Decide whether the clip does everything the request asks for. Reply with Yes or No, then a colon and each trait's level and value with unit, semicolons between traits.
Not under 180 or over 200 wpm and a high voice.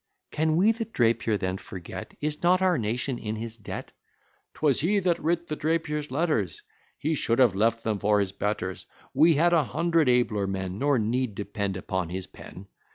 No: average, 185 wpm; low, 120 Hz